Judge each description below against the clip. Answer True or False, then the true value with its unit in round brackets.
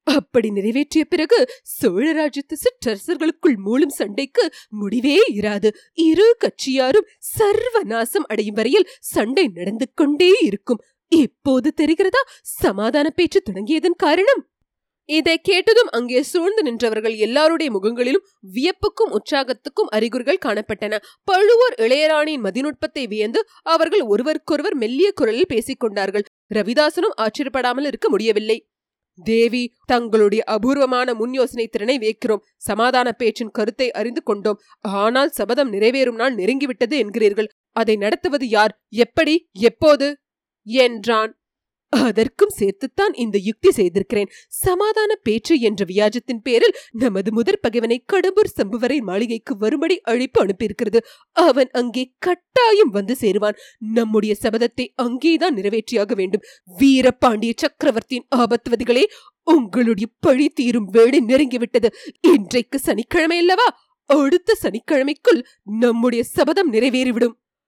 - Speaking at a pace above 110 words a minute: False (100 wpm)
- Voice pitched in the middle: False (255 Hz)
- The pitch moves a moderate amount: False (6.5 semitones)